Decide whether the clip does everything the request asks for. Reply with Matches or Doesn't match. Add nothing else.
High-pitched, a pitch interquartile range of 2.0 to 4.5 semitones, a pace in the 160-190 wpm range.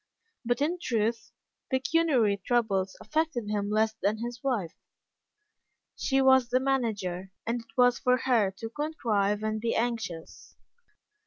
Doesn't match